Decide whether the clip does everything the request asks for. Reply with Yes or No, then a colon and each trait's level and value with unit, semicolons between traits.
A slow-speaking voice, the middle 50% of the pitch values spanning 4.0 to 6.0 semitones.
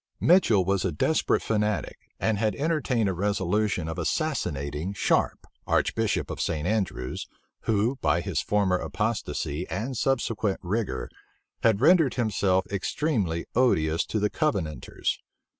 Yes: slow, 125 wpm; average, 4.6 semitones